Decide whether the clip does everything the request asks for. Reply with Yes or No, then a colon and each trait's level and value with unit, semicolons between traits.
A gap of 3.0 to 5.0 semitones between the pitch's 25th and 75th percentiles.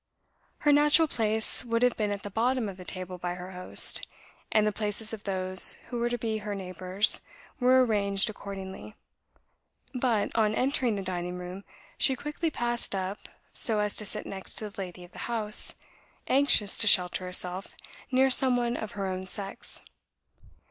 Yes: average, 4.1 semitones